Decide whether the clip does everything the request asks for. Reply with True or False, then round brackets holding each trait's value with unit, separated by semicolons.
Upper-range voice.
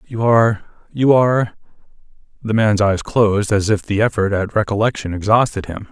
False (105 Hz)